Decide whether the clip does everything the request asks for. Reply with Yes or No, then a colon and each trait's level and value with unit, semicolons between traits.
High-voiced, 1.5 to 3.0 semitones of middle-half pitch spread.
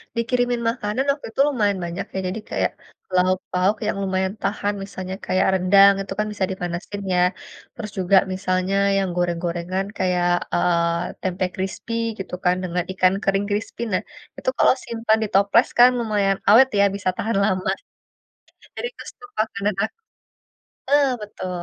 Yes: high, 195 Hz; narrow, 2.6 semitones